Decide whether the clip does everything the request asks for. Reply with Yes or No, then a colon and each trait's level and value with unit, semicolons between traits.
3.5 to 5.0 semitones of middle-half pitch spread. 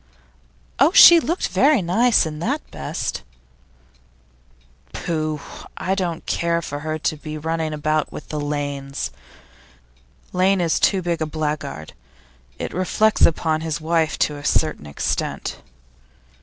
No: average, 3.1 semitones